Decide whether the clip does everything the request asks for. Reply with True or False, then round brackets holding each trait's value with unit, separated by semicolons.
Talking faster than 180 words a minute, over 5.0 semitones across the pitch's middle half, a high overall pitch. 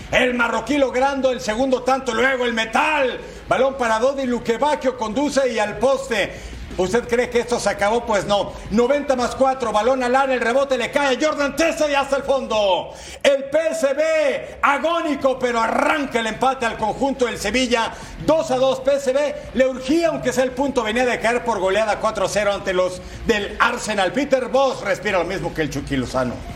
False (190 wpm; 3.6 semitones; 255 Hz)